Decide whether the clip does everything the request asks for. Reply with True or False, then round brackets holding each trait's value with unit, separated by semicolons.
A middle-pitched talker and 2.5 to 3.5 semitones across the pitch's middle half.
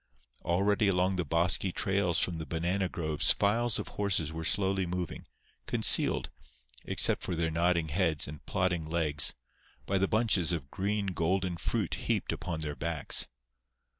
False (90 Hz; 3.1 semitones)